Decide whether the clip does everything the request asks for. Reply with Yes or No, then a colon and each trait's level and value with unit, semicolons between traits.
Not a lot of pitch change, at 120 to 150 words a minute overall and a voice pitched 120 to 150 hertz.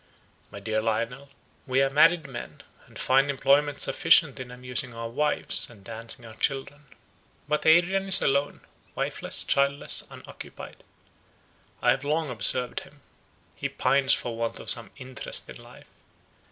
No: average, 3.5 semitones; average, 145 wpm; low, 135 Hz